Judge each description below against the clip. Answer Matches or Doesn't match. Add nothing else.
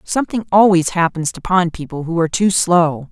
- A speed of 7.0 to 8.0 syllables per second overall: Doesn't match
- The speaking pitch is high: Doesn't match